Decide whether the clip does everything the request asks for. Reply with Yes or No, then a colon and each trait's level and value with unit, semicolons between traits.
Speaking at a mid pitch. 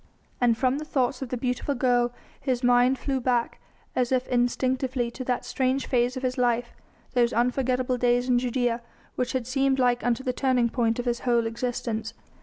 No: very high, 250 Hz